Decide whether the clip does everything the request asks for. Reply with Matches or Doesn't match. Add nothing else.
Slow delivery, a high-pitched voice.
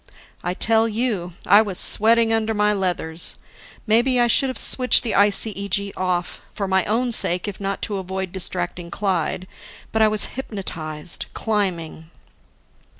Doesn't match